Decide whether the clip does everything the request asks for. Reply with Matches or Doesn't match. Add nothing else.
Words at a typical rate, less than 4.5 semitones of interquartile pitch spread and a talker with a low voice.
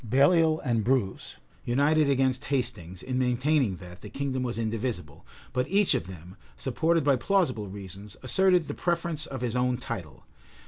Doesn't match